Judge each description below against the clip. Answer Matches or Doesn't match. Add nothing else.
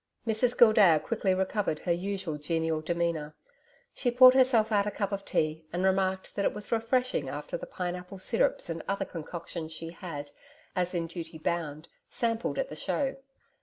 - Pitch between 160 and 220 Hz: Matches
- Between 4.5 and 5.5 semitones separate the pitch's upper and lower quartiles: Matches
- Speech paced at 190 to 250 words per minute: Doesn't match